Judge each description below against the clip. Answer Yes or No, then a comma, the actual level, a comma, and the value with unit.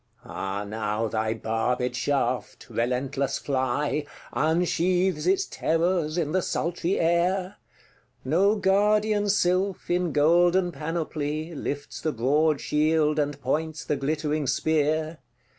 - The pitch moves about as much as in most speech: Yes, average, 4.1 semitones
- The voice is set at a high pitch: No, medium, 155 Hz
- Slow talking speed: Yes, slow, 110 wpm